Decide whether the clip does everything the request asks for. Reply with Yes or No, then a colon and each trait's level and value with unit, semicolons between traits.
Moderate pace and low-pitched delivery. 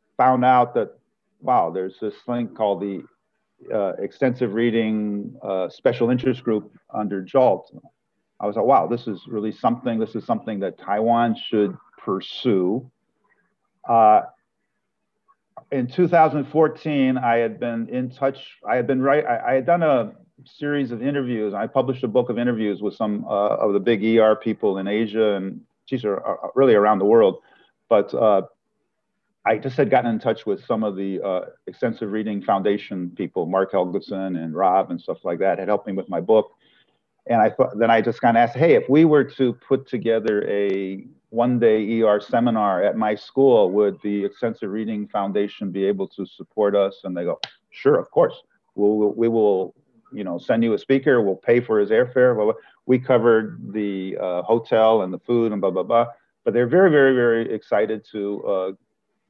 Yes: average, 185 wpm; low, 115 Hz